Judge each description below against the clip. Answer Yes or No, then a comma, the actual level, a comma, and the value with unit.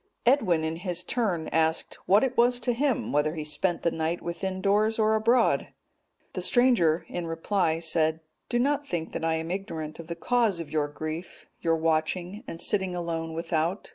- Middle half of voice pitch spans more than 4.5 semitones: Yes, average, 4.9 semitones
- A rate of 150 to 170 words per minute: No, average, 185 wpm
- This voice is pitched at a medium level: Yes, medium, 170 Hz